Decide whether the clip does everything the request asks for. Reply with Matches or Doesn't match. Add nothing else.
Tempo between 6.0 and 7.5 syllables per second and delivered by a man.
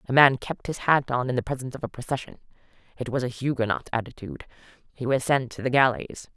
Doesn't match